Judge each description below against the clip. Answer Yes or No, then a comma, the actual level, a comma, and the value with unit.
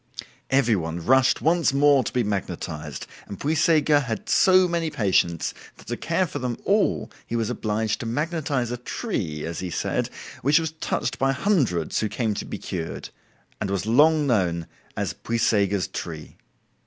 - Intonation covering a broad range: Yes, wide, 7.3 semitones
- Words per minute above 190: No, average, 165 wpm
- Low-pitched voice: Yes, low, 120 Hz